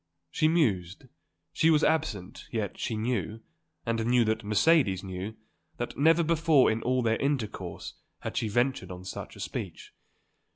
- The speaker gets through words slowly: No, average, 155 wpm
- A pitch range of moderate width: No, wide, 5.9 semitones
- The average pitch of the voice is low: Yes, low, 115 Hz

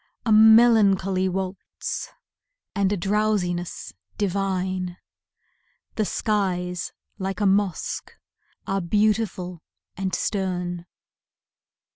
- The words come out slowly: Yes, slow, 80 wpm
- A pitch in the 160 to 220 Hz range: Yes, high, 190 Hz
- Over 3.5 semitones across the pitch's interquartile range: No, narrow, 2.4 semitones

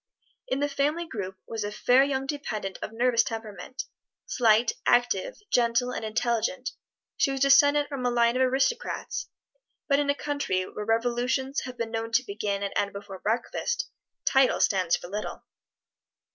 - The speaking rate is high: No, average, 160 wpm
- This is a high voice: Yes, high, 245 Hz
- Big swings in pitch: No, average, 4.1 semitones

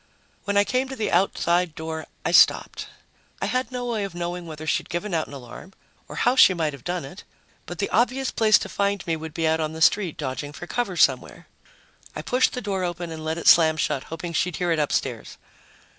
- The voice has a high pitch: No, medium, 175 Hz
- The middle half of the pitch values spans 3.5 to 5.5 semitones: Yes, average, 4.1 semitones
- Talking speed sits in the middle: No, fast, 225 wpm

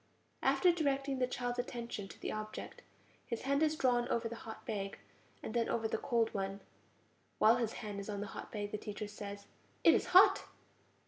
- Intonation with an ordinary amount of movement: Yes, average, 3.2 semitones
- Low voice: No, high, 230 Hz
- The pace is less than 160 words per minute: No, average, 195 wpm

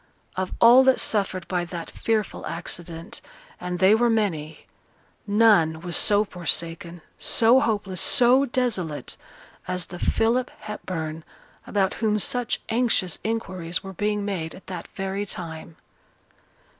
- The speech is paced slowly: Yes, slow, 130 wpm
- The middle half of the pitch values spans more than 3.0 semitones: Yes, average, 4.5 semitones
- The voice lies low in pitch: No, high, 190 Hz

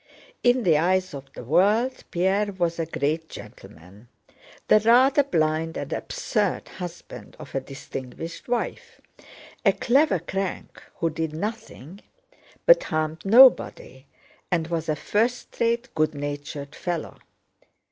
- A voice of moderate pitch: Yes, medium, 170 Hz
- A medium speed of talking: No, slow, 125 wpm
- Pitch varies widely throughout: Yes, wide, 6.1 semitones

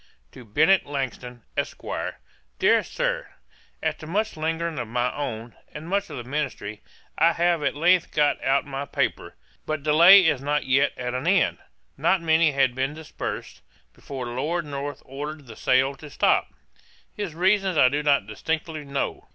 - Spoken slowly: No, average, 165 wpm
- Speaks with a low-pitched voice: No, medium, 145 Hz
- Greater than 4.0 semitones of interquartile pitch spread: No, average, 3.7 semitones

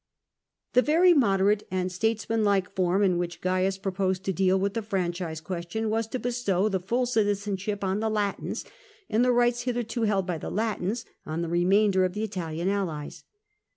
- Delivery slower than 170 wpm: No, average, 175 wpm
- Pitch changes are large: No, average, 3.2 semitones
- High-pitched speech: Yes, high, 195 Hz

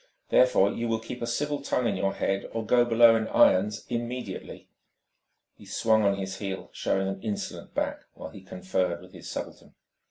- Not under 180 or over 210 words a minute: Yes, average, 185 wpm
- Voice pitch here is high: No, low, 110 Hz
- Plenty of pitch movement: No, average, 3.5 semitones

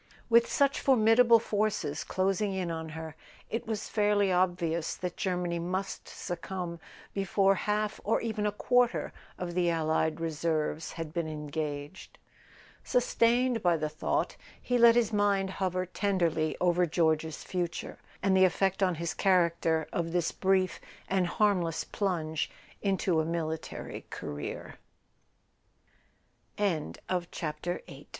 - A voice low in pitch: No, medium, 185 Hz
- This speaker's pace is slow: Yes, slow, 110 wpm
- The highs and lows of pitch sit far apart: No, average, 4.0 semitones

